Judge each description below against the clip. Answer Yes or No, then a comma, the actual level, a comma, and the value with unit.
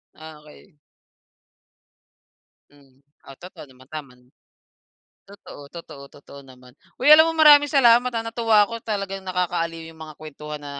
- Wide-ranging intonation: Yes, wide, 7.6 semitones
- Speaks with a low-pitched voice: No, medium, 165 Hz